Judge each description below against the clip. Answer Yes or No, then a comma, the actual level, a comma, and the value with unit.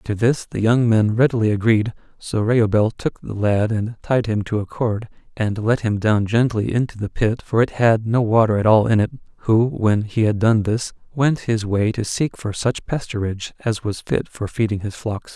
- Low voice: Yes, low, 110 Hz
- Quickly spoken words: Yes, fast, 220 wpm